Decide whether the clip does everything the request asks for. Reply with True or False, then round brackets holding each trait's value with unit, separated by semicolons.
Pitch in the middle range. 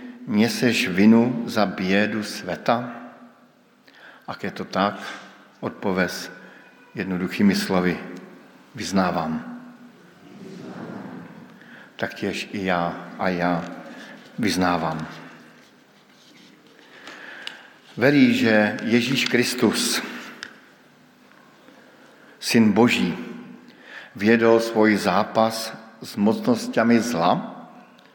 False (115 Hz)